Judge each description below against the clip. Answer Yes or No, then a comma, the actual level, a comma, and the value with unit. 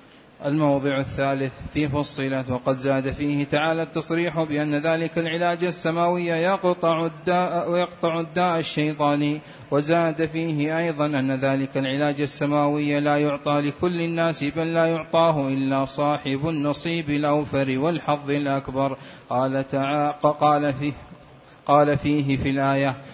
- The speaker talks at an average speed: Yes, average, 120 wpm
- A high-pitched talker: No, medium, 145 Hz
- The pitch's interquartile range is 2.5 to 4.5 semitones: Yes, average, 2.9 semitones